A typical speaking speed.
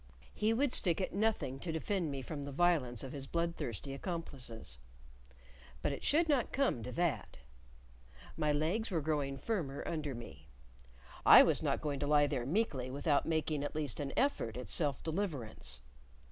Yes: average, 170 wpm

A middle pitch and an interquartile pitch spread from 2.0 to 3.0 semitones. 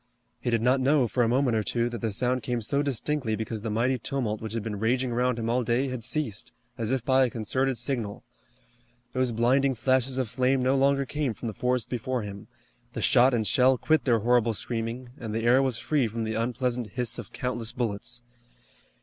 No: low, 120 Hz; narrow, 2.4 semitones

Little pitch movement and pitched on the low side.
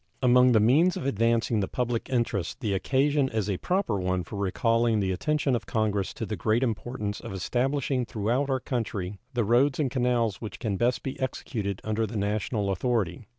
No: average, 3.8 semitones; low, 115 Hz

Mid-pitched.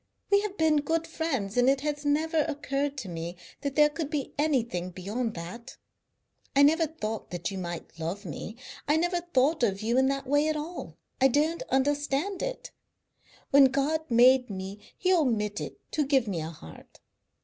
No: very high, 275 Hz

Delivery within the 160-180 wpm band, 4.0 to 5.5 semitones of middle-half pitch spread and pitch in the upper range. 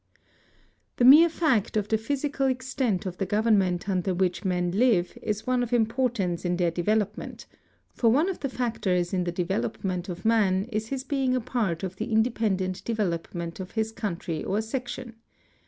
Yes: average, 175 wpm; average, 5.2 semitones; high, 215 Hz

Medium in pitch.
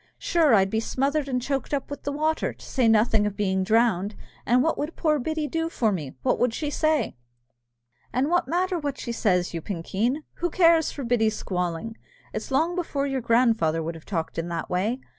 No: high, 245 Hz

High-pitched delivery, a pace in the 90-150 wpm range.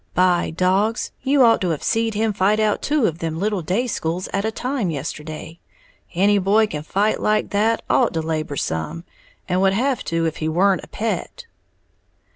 No: high, 195 Hz; average, 190 wpm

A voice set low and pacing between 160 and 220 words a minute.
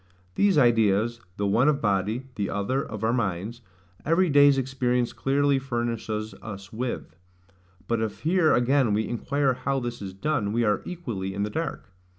Yes: low, 120 Hz; average, 165 wpm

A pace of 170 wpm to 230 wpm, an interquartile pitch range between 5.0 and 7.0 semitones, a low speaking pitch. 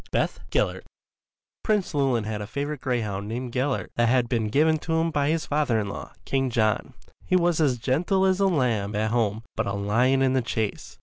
Yes: fast, 205 wpm; wide, 5.4 semitones; low, 130 Hz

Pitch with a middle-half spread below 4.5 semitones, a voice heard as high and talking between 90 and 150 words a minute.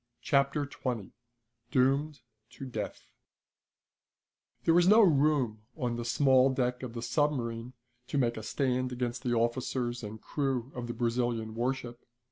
No: narrow, 2.5 semitones; low, 125 Hz; average, 140 wpm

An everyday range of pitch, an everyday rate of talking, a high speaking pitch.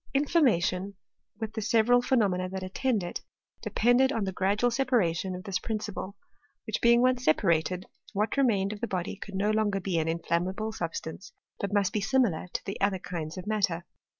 Yes: average, 3.6 semitones; average, 180 wpm; high, 200 Hz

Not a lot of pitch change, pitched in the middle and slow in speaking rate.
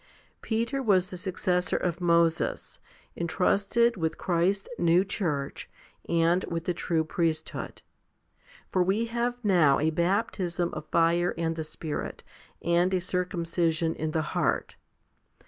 Yes: narrow, 2.3 semitones; medium, 175 Hz; slow, 130 wpm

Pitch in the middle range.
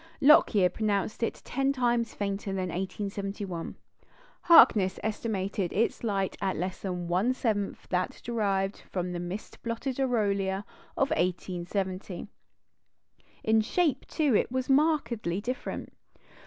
No: high, 205 Hz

